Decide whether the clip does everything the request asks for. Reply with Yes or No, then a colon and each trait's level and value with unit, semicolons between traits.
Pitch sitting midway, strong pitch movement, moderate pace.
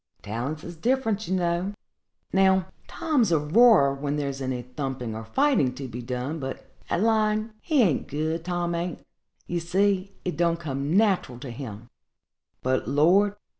Yes: medium, 170 Hz; wide, 6.5 semitones; average, 160 wpm